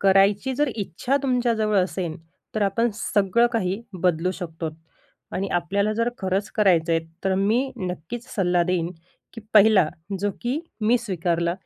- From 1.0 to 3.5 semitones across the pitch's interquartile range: No, average, 4.0 semitones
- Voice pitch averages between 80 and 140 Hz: No, high, 195 Hz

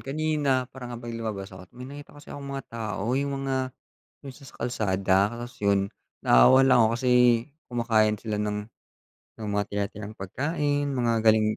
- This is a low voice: Yes, low, 120 Hz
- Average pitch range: Yes, average, 4.2 semitones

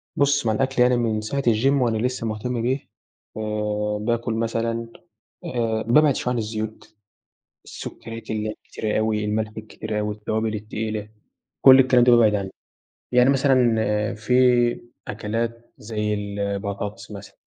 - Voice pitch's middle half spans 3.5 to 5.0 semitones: No, narrow, 2.4 semitones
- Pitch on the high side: No, low, 110 Hz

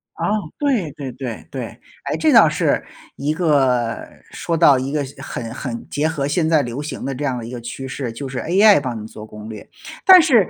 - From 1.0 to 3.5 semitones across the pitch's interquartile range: No, average, 4.6 semitones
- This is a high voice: No, low, 135 Hz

